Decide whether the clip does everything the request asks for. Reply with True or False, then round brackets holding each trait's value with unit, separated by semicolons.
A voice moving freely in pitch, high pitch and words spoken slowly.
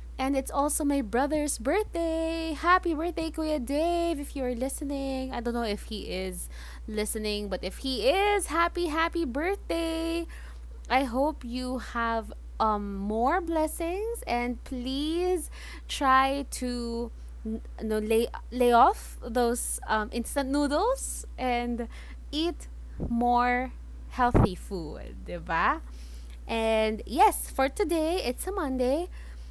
True (6.2 semitones; 265 Hz; 120 wpm)